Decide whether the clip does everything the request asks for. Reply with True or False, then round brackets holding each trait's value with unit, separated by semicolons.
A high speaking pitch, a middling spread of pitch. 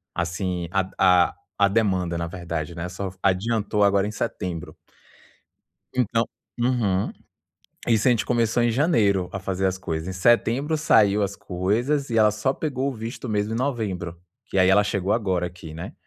False (100 Hz; 4.0 semitones)